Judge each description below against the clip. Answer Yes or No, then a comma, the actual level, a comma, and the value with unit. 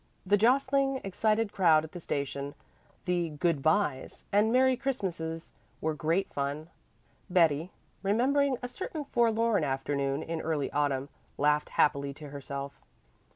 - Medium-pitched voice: Yes, medium, 165 Hz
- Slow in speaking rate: Yes, slow, 130 wpm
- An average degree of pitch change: No, wide, 7.5 semitones